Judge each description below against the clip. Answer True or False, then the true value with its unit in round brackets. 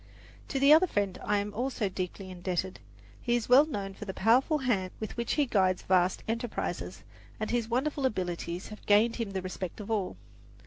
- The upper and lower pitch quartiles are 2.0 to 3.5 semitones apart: False (4.4 semitones)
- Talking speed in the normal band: True (195 wpm)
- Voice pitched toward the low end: False (210 Hz)